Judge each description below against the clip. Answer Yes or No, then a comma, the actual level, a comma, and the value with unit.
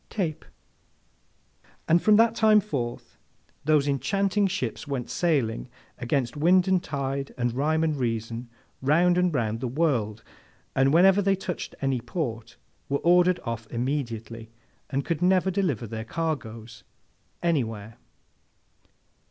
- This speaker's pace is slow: Yes, slow, 130 wpm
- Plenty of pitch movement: Yes, wide, 7.0 semitones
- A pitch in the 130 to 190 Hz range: Yes, medium, 140 Hz